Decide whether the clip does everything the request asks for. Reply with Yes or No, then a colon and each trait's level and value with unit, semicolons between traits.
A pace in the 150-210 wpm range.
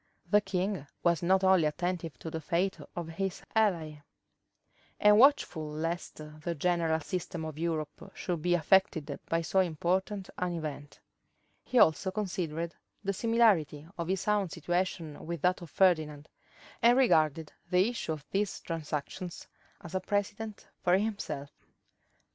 No: average, 140 wpm